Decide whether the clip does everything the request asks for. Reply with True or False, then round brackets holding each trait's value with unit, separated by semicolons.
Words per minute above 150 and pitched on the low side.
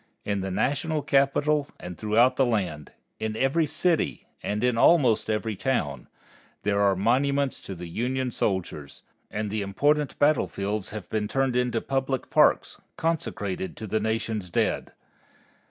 False (145 wpm; 115 Hz)